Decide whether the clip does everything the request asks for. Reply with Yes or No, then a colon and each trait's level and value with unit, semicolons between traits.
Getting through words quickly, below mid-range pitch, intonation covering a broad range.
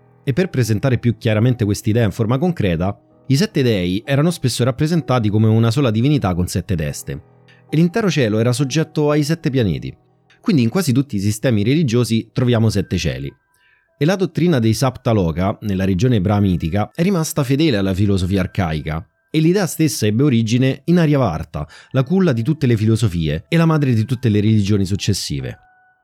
Yes: fast, 175 wpm; low, 125 Hz; wide, 6.2 semitones